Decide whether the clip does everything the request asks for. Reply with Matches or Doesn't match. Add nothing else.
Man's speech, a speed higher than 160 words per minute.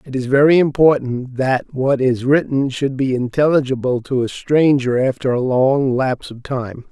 Matches